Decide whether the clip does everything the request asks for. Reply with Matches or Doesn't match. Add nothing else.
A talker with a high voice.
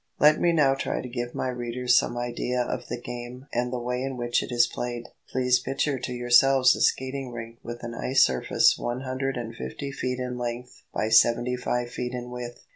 Doesn't match